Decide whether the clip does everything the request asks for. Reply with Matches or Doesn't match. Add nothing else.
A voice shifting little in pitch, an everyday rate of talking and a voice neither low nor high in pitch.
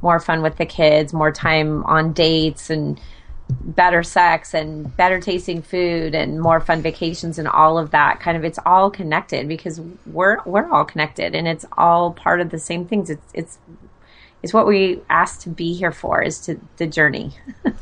Matches